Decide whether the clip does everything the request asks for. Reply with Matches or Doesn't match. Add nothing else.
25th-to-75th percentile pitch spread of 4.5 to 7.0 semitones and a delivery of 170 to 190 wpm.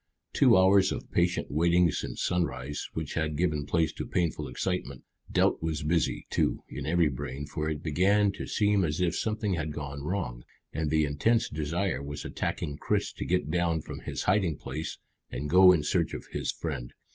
Doesn't match